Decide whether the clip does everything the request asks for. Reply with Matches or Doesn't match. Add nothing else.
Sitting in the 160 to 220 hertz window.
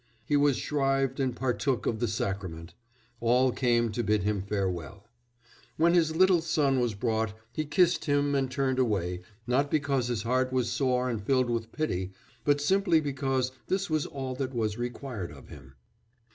Doesn't match